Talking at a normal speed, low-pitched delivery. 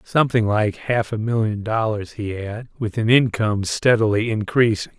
Yes: average, 155 wpm; low, 110 Hz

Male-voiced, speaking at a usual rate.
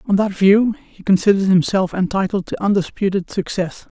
Yes: male; average, 150 wpm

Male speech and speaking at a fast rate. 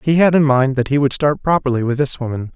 Yes: male; fast, 280 wpm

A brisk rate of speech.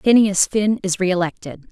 No: average, 140 wpm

